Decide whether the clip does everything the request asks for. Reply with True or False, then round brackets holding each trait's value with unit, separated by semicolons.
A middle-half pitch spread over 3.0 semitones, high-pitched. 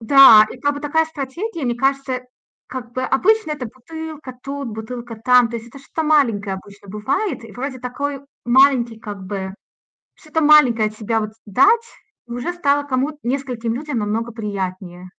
True (4.4 semitones; 250 Hz)